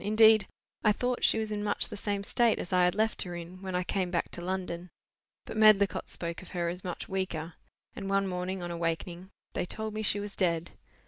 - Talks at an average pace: No, fast, 220 wpm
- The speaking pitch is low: No, high, 190 Hz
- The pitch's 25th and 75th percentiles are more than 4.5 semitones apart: No, average, 2.9 semitones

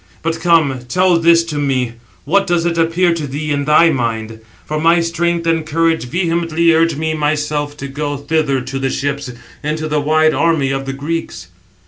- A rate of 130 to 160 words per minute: No, average, 185 wpm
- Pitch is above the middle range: No, medium, 155 Hz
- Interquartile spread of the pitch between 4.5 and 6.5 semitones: No, average, 2.8 semitones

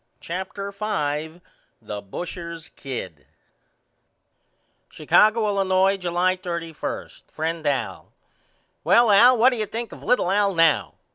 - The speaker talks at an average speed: No, slow, 115 wpm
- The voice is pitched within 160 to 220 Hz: Yes, medium, 185 Hz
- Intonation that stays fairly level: No, average, 4.1 semitones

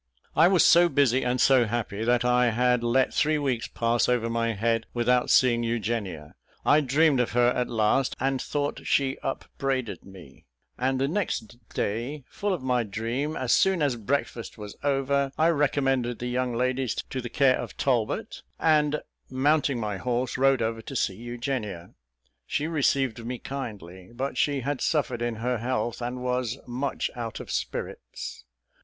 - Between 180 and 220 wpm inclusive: No, average, 170 wpm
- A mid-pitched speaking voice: No, low, 125 Hz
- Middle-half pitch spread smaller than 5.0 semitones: Yes, average, 2.8 semitones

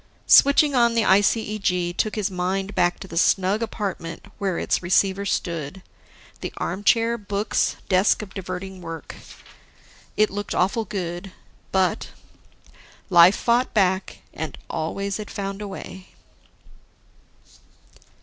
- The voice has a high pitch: Yes, high, 195 Hz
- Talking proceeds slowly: Yes, slow, 120 wpm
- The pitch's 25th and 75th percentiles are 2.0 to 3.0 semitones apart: Yes, narrow, 2.6 semitones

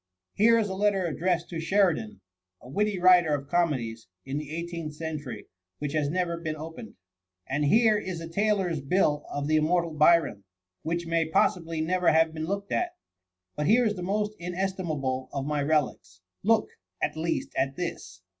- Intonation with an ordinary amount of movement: Yes, average, 3.9 semitones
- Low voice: No, medium, 165 Hz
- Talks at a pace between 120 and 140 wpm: No, average, 180 wpm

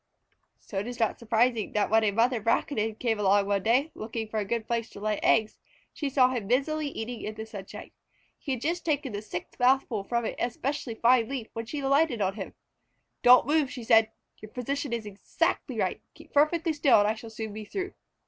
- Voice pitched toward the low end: No, high, 230 Hz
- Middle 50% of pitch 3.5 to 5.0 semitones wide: Yes, average, 3.8 semitones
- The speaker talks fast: Yes, fast, 215 wpm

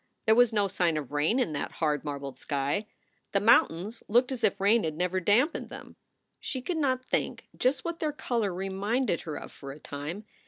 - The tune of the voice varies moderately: No, wide, 7.8 semitones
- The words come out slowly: No, average, 200 wpm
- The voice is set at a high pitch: Yes, high, 200 Hz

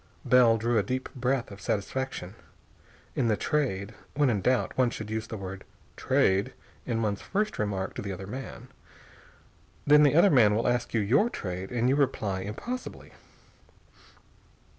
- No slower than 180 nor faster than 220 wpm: No, average, 160 wpm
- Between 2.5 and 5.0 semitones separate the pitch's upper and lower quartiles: Yes, average, 4.6 semitones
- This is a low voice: Yes, low, 115 Hz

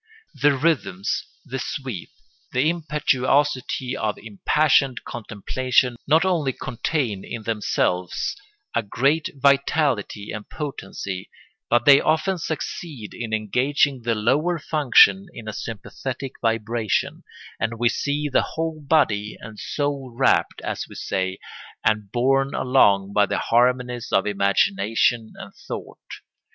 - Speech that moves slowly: Yes, slow, 120 wpm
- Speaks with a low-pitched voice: Yes, low, 125 Hz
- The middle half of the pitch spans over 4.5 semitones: Yes, average, 4.9 semitones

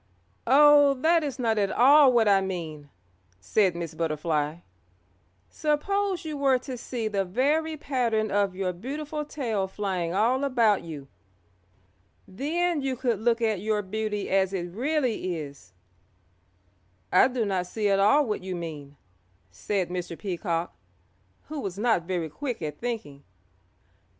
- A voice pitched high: Yes, high, 210 Hz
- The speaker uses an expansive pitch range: Yes, wide, 6.8 semitones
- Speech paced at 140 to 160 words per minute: Yes, average, 145 wpm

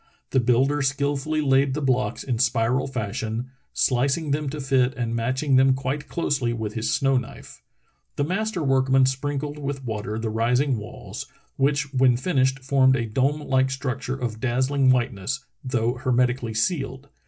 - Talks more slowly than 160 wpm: No, average, 165 wpm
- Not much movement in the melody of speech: Yes, narrow, 2.2 semitones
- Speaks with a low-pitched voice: Yes, low, 130 Hz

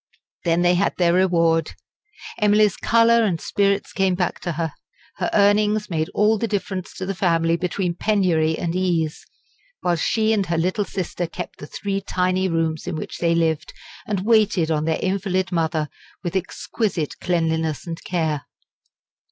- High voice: No, medium, 180 Hz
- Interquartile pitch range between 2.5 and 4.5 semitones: Yes, average, 3.2 semitones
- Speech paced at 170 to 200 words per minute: No, average, 155 wpm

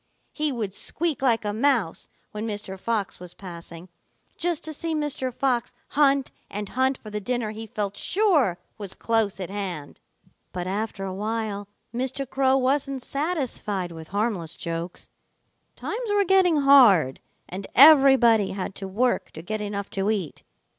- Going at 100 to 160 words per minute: Yes, average, 155 wpm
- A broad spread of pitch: Yes, wide, 5.8 semitones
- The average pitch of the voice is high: Yes, high, 220 Hz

